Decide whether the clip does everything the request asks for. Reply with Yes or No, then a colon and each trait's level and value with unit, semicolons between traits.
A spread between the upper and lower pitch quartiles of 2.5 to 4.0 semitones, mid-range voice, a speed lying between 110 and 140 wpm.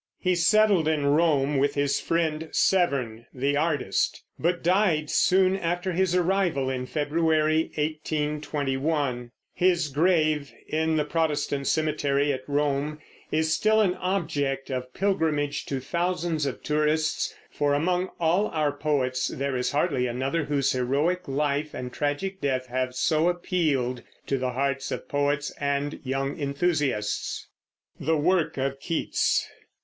Yes: average, 3.4 semitones; medium, 150 Hz; slow, 135 wpm